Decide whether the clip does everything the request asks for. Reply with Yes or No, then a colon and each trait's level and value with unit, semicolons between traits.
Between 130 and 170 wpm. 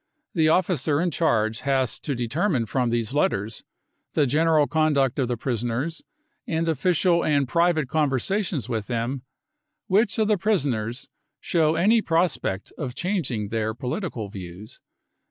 Yes: average, 140 wpm